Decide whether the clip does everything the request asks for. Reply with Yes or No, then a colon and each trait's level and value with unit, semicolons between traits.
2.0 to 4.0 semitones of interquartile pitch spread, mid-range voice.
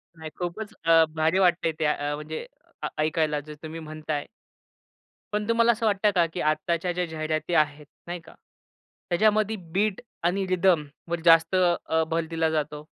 Yes: average, 2.9 semitones; medium, 165 Hz